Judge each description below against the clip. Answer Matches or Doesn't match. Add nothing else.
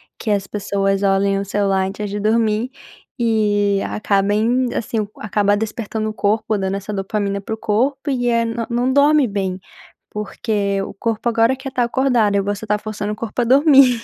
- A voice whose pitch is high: Matches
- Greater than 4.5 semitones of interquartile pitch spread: Doesn't match